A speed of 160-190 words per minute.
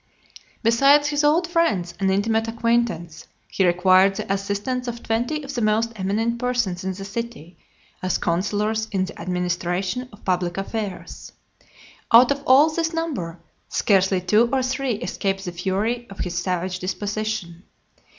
No: average, 150 wpm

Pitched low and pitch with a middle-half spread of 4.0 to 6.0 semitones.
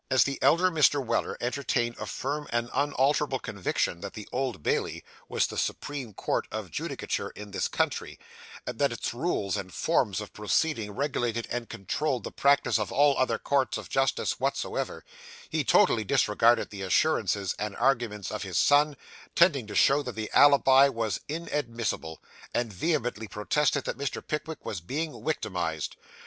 Yes: low, 120 Hz; average, 5.3 semitones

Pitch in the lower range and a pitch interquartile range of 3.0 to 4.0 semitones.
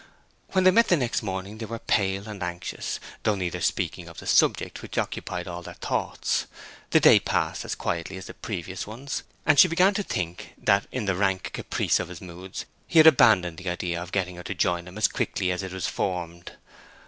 Yes: very low, 95 Hz; average, 3.6 semitones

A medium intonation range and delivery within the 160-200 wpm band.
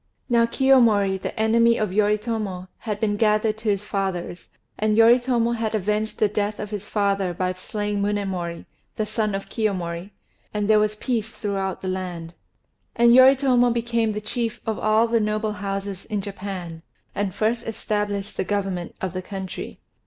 No: narrow, 2.3 semitones; average, 165 wpm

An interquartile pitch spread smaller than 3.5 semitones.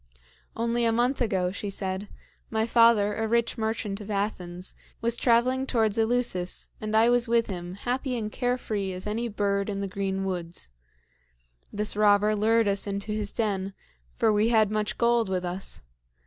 Yes: average, 2.8 semitones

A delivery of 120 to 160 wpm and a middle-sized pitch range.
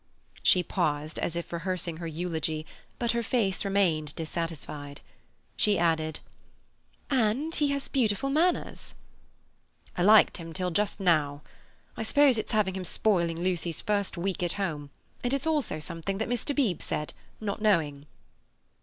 Yes: average, 145 wpm; average, 5.0 semitones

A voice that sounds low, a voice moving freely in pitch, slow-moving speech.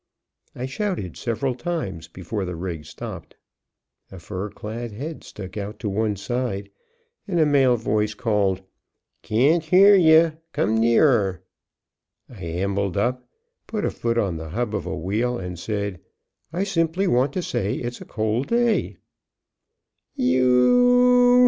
No: low, 115 Hz; wide, 7.8 semitones; average, 145 wpm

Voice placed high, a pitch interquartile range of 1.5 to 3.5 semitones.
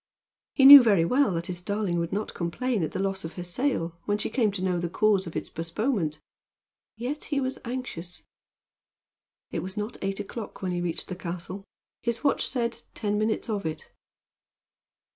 No: high, 195 Hz; average, 5.0 semitones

